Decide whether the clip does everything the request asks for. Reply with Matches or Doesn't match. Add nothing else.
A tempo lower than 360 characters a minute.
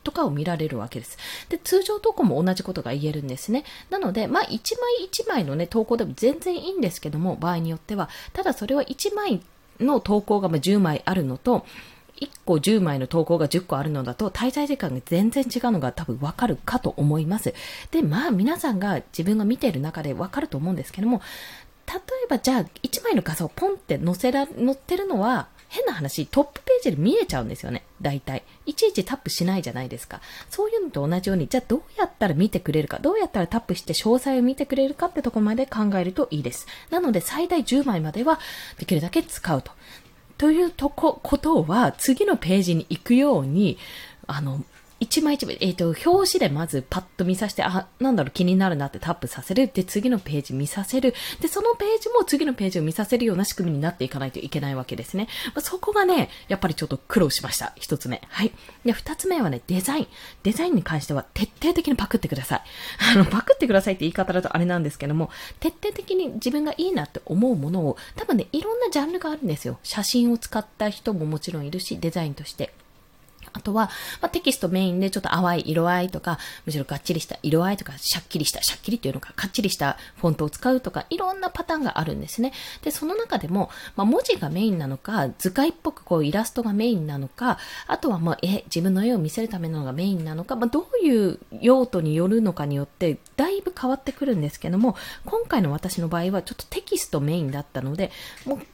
Doesn't match